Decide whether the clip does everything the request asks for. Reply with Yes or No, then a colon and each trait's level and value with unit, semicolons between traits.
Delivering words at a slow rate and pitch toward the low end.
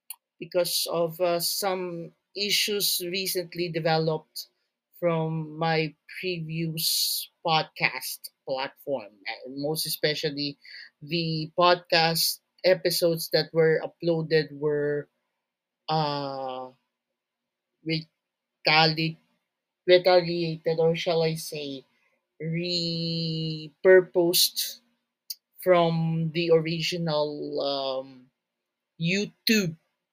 No: slow, 70 wpm; medium, 165 Hz